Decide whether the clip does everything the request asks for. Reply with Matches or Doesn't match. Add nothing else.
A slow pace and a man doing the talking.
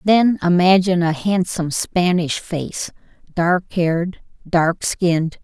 Doesn't match